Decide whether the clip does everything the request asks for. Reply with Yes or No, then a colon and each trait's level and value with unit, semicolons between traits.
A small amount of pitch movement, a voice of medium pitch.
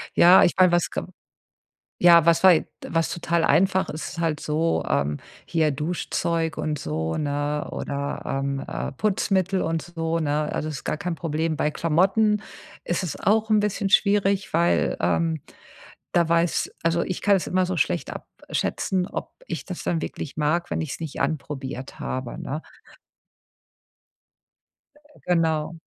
No: average, 3.0 semitones; medium, 165 Hz